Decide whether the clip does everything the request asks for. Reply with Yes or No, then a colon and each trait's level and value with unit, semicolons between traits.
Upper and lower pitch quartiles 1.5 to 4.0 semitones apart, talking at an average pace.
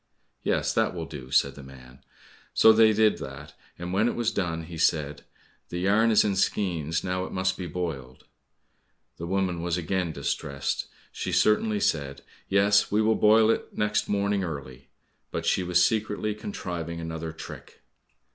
No: average, 4.5 semitones; average, 165 wpm